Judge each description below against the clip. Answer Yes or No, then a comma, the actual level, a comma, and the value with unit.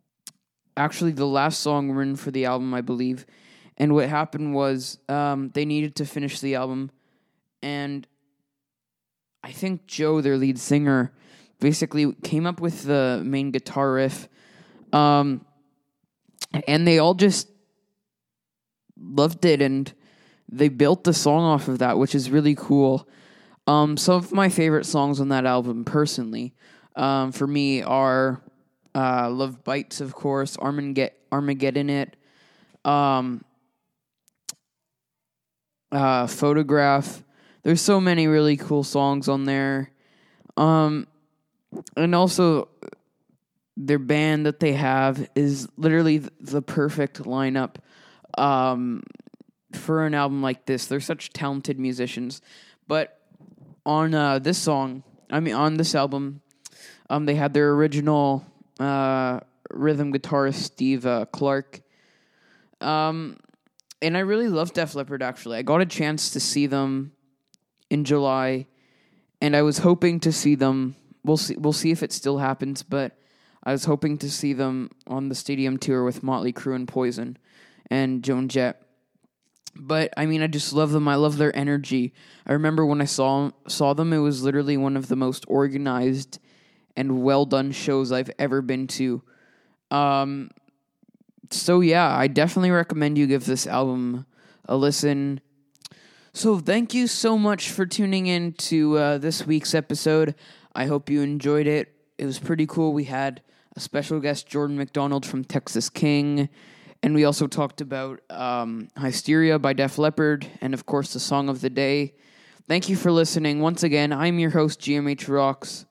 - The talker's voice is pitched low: No, medium, 145 Hz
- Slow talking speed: No, average, 150 wpm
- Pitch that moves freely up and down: No, narrow, 2.4 semitones